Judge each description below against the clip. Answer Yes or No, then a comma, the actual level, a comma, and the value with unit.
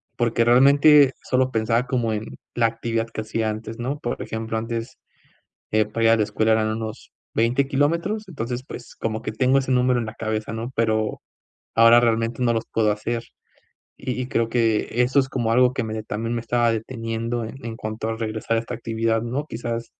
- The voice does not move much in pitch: Yes, narrow, 1.8 semitones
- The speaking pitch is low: Yes, low, 115 Hz